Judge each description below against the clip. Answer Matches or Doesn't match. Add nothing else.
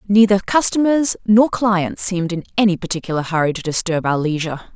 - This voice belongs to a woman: Matches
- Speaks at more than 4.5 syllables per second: Matches